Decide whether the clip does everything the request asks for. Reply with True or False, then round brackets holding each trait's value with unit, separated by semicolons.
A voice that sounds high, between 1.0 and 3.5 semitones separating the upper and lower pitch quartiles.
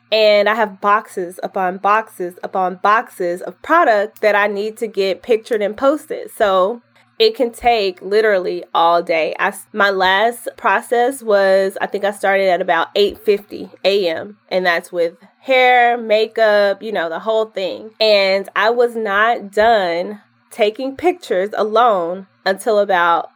True (205 Hz; 3.2 semitones)